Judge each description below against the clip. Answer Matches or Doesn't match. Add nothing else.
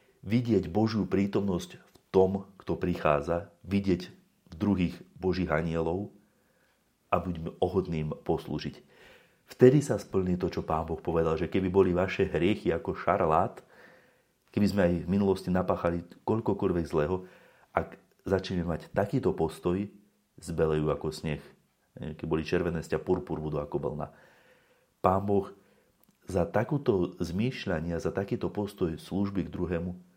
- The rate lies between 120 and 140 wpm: Matches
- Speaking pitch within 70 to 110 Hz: Matches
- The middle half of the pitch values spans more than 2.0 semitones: Matches